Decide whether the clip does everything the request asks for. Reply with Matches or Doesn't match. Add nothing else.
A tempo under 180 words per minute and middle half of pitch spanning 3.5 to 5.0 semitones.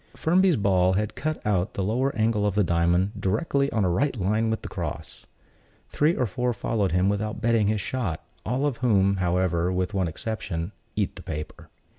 Doesn't match